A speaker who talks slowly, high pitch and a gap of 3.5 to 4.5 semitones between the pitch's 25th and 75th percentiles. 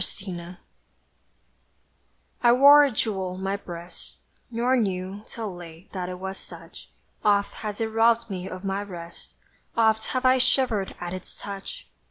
No: average, 155 wpm; high, 200 Hz; average, 3.9 semitones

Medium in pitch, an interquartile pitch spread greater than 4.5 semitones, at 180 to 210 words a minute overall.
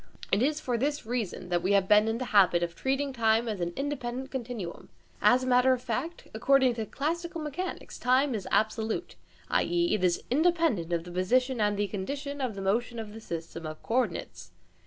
No: high, 235 Hz; wide, 5.4 semitones; average, 200 wpm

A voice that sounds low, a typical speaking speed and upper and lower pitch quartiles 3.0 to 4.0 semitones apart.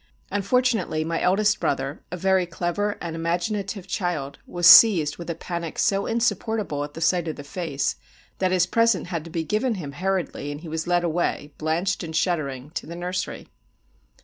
No: medium, 175 Hz; average, 180 wpm; average, 3.4 semitones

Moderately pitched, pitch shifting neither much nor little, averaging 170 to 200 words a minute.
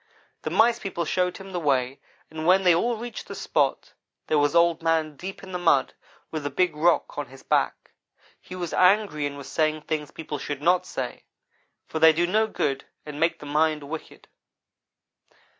Yes: medium, 160 Hz; average, 3.5 semitones; average, 190 wpm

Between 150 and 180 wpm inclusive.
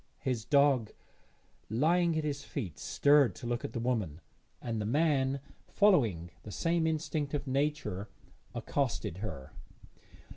No: slow, 135 wpm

